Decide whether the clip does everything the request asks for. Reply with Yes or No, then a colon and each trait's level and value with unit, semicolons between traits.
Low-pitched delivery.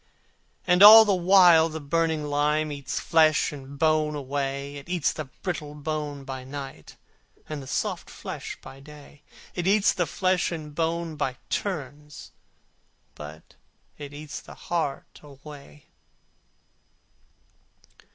No: medium, 150 Hz